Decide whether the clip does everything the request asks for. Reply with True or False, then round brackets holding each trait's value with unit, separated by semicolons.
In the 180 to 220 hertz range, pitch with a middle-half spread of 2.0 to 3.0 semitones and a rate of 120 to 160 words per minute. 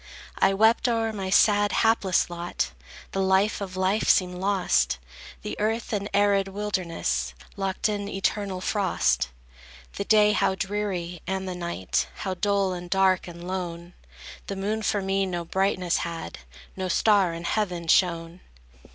True (190 Hz; 2.5 semitones; 150 wpm)